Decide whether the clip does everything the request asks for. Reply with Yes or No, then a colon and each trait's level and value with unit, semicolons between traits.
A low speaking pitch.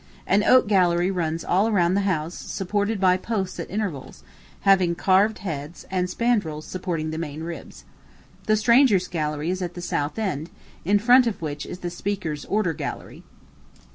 No: medium, 185 Hz